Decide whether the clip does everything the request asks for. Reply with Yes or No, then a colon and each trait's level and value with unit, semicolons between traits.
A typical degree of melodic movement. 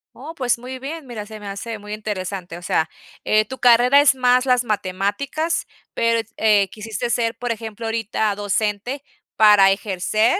Yes: average, 3.3 semitones